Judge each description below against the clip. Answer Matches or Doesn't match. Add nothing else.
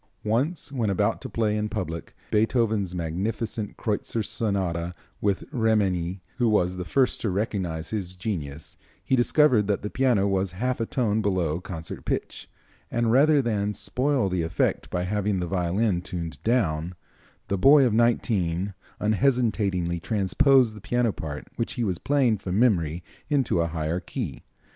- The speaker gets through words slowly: Doesn't match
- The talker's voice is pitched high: Doesn't match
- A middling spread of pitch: Matches